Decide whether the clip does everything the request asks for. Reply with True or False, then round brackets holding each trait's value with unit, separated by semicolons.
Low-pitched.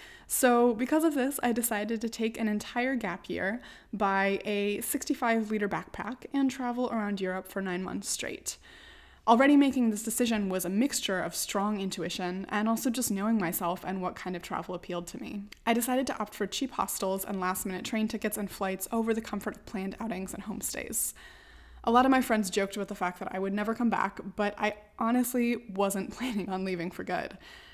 False (210 Hz)